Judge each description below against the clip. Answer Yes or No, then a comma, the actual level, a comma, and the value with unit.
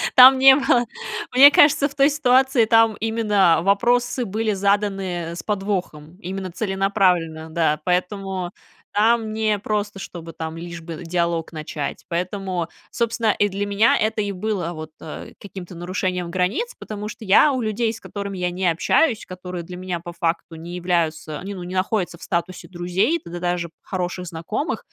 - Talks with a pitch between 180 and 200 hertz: Yes, high, 190 Hz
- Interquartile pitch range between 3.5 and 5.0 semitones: Yes, average, 3.9 semitones